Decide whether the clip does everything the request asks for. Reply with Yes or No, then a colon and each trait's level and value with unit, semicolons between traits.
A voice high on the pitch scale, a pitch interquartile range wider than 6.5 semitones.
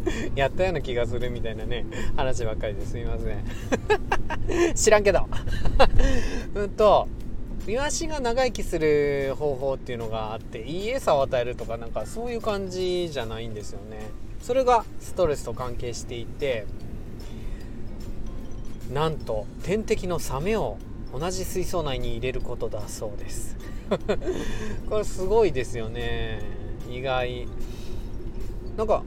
No: low, 120 Hz; wide, 6.9 semitones